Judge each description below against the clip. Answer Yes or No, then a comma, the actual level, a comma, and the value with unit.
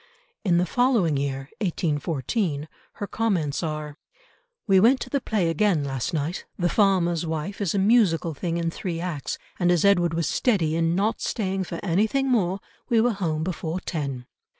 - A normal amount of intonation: Yes, average, 4.1 semitones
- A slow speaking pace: No, average, 175 wpm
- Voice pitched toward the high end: No, medium, 175 Hz